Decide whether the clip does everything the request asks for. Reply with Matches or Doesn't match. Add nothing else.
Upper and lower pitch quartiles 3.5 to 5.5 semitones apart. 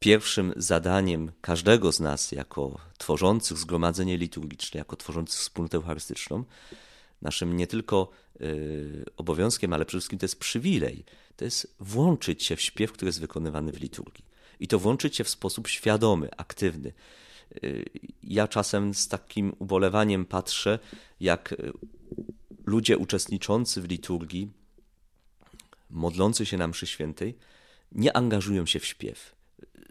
Matches